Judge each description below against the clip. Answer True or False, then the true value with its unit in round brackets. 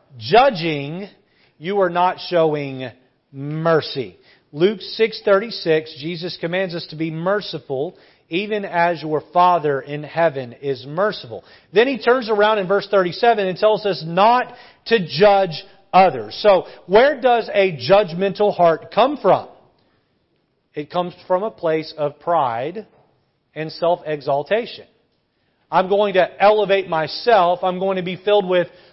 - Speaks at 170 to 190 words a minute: False (135 wpm)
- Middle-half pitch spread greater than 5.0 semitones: False (4.3 semitones)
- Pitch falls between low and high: True (180 Hz)